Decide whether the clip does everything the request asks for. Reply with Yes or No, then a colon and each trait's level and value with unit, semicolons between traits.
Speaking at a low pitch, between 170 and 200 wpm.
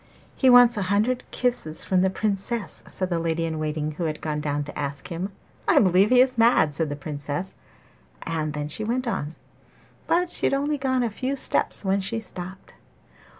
No: high, 190 Hz; average, 195 wpm